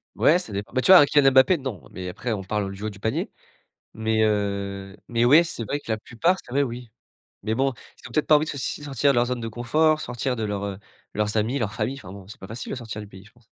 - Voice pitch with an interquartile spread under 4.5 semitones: No, average, 4.8 semitones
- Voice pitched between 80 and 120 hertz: Yes, low, 115 Hz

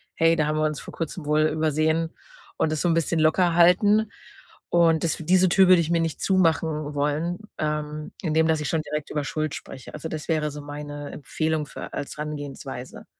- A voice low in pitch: No, medium, 155 Hz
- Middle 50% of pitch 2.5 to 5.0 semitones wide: No, narrow, 1.7 semitones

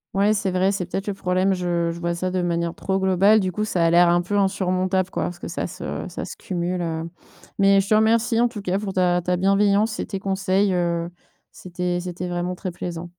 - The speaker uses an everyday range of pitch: No, narrow, 2.0 semitones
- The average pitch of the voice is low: No, medium, 185 Hz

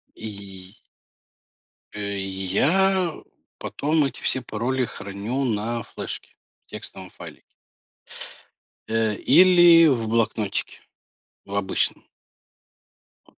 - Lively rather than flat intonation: Yes, wide, 6.0 semitones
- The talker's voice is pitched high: No, low, 115 Hz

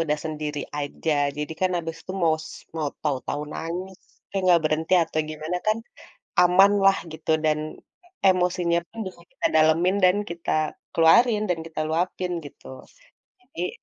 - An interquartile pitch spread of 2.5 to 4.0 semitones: Yes, average, 2.9 semitones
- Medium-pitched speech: Yes, medium, 165 Hz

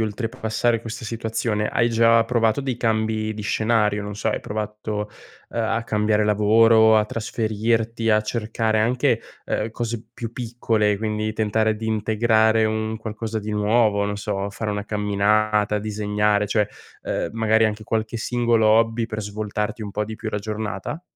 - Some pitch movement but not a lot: No, narrow, 1.2 semitones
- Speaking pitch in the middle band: No, low, 110 Hz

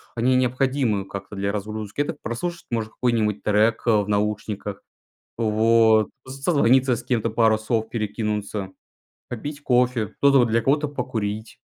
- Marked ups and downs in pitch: No, average, 3.0 semitones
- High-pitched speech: No, low, 115 Hz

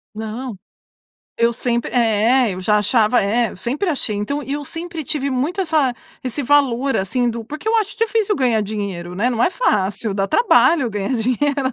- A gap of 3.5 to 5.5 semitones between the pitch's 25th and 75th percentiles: Yes, average, 5.2 semitones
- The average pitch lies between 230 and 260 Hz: Yes, high, 245 Hz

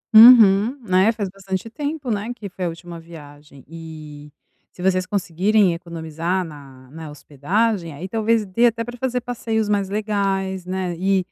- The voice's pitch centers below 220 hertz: Yes, high, 190 Hz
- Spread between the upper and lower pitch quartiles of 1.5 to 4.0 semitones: No, average, 4.7 semitones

